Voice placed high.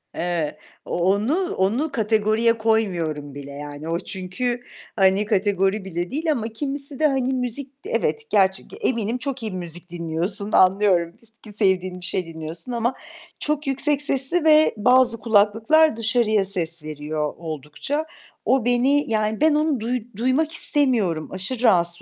Yes: high, 215 Hz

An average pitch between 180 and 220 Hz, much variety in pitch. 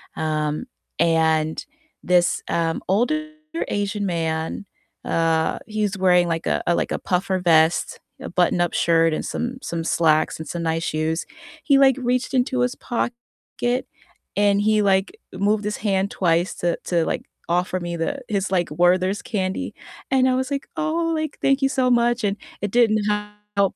Yes: high, 190 Hz; wide, 6.2 semitones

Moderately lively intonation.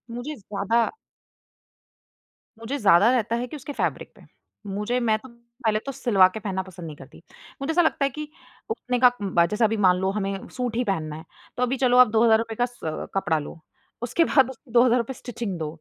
Yes: average, 4.2 semitones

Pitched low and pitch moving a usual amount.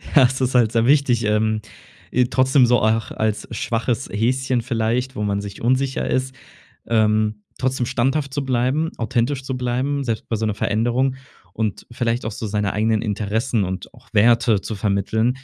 Yes: low, 120 Hz; average, 3.1 semitones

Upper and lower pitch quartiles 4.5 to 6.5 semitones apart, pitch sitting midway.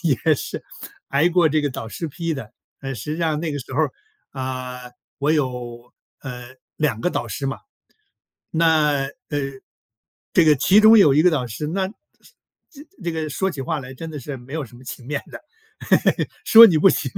No: average, 4.1 semitones; medium, 150 Hz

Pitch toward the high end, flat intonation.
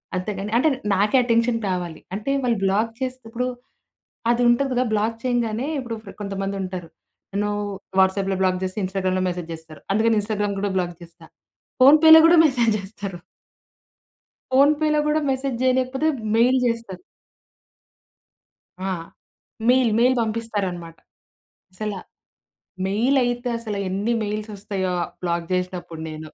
No: high, 215 Hz; average, 4.6 semitones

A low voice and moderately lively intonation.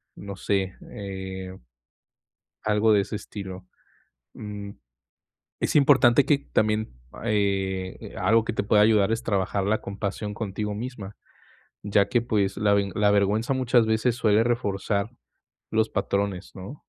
No: low, 105 Hz; narrow, 2.0 semitones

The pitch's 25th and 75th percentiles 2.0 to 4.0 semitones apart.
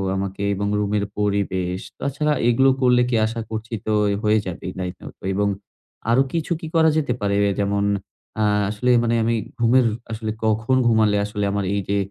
Yes: average, 2.8 semitones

